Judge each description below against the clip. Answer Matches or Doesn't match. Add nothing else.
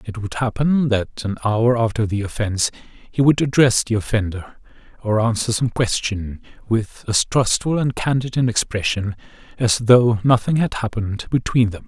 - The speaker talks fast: Doesn't match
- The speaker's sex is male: Matches